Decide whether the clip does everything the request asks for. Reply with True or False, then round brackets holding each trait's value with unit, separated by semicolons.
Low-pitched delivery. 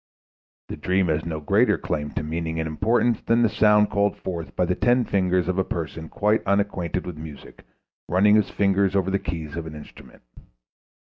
True (90 Hz)